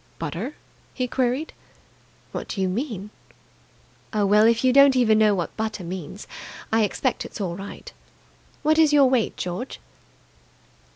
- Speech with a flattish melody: No, average, 4.9 semitones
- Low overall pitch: No, high, 220 Hz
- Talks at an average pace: Yes, average, 150 wpm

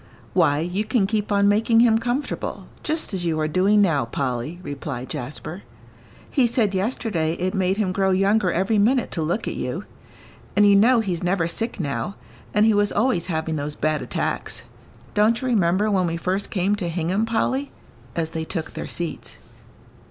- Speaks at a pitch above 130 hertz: Yes, high, 190 Hz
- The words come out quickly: No, average, 180 wpm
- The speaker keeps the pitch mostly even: No, average, 4.6 semitones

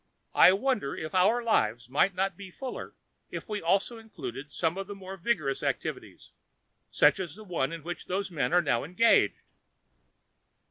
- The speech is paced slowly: No, average, 170 wpm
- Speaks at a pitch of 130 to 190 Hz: Yes, medium, 185 Hz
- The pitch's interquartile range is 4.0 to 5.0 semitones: Yes, average, 4.5 semitones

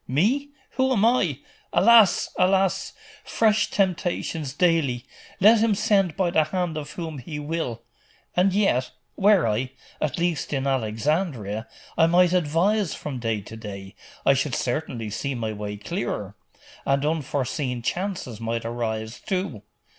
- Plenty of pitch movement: Yes, wide, 7.6 semitones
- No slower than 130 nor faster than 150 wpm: Yes, average, 140 wpm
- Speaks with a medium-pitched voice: Yes, medium, 155 Hz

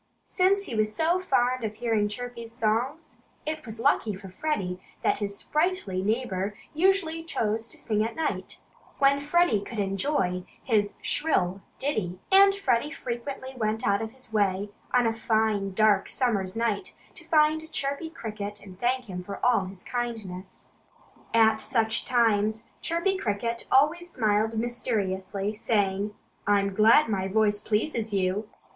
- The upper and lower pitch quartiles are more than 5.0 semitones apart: No, average, 4.6 semitones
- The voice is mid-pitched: No, high, 225 Hz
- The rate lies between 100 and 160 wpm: Yes, average, 150 wpm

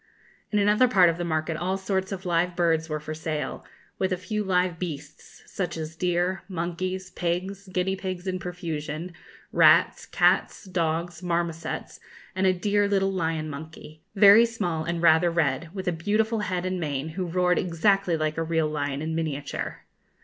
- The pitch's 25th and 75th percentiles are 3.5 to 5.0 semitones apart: No, average, 2.8 semitones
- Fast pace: No, average, 170 wpm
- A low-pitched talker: No, medium, 175 Hz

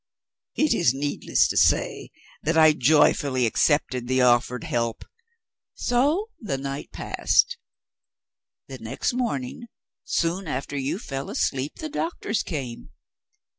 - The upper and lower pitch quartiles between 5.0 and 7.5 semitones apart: Yes, wide, 5.6 semitones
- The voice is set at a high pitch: No, medium, 140 Hz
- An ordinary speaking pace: No, slow, 120 wpm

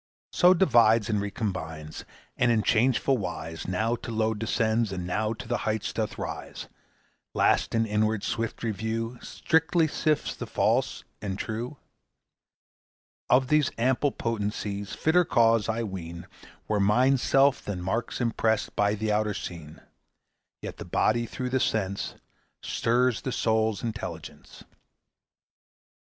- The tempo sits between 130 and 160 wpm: Yes, slow, 135 wpm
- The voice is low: Yes, low, 110 Hz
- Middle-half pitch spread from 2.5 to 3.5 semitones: Yes, average, 2.9 semitones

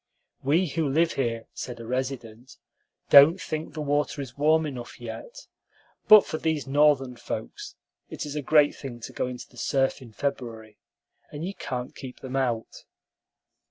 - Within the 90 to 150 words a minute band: No, average, 165 wpm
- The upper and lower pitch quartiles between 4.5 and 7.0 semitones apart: No, average, 3.4 semitones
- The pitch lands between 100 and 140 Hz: Yes, low, 135 Hz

